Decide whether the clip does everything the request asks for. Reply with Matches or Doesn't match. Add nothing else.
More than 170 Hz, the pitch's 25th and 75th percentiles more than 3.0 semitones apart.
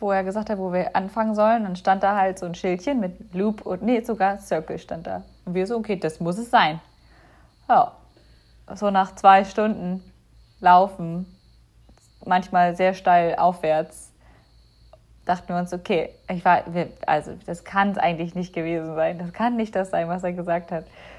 Doesn't match